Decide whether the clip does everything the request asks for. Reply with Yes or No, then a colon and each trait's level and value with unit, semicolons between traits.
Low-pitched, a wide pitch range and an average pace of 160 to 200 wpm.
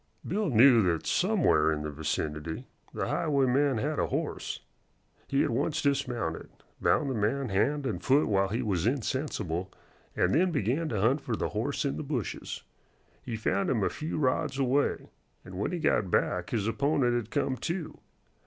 Yes: low, 125 Hz; wide, 6.2 semitones; average, 175 wpm